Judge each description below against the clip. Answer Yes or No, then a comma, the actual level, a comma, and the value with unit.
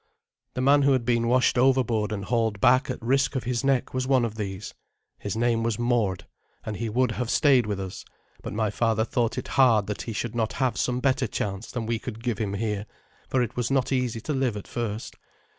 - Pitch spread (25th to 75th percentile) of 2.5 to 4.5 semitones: Yes, average, 2.8 semitones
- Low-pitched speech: Yes, low, 120 Hz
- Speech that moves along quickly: Yes, fast, 225 wpm